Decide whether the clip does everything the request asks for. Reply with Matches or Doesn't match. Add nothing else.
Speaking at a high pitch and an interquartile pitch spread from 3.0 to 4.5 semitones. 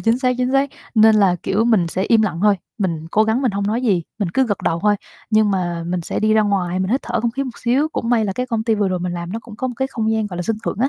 Matches